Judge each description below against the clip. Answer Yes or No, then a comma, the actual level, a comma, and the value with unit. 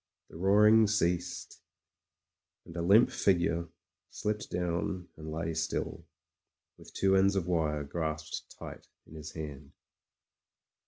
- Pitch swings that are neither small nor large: Yes, average, 3.4 semitones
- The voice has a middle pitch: No, very low, 85 Hz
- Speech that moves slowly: Yes, slow, 120 wpm